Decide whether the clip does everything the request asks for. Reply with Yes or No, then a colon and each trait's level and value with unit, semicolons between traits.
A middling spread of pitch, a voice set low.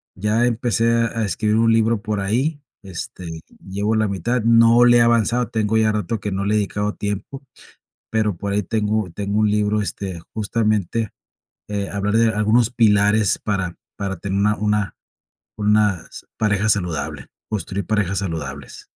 No: narrow, 2.1 semitones; low, 105 Hz